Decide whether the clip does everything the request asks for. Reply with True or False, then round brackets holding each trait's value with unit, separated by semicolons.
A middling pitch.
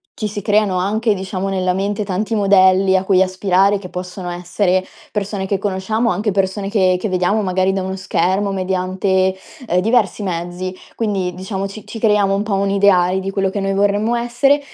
False (195 Hz)